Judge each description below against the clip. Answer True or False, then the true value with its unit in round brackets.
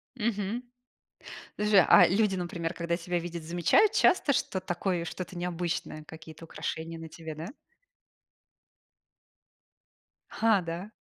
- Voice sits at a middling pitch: True (175 Hz)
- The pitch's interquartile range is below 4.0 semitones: True (3.0 semitones)